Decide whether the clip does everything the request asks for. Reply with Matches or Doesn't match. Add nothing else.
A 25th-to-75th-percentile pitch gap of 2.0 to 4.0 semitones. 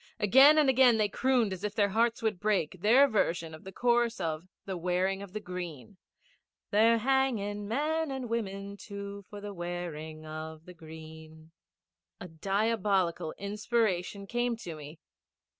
Doesn't match